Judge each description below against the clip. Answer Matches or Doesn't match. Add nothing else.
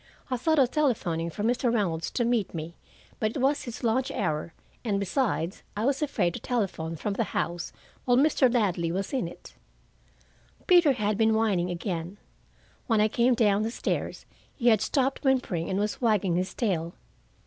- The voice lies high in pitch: Matches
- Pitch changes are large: Matches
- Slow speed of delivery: Doesn't match